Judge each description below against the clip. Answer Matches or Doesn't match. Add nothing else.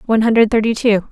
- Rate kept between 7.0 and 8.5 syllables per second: Matches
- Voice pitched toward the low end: Doesn't match